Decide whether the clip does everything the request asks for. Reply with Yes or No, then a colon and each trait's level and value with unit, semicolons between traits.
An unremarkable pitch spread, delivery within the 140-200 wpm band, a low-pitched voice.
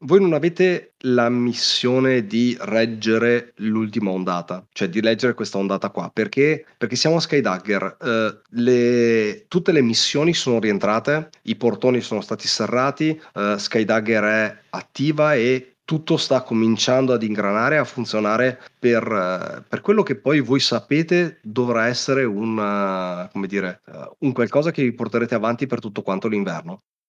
Yes: average, 3.8 semitones; average, 150 wpm; low, 120 Hz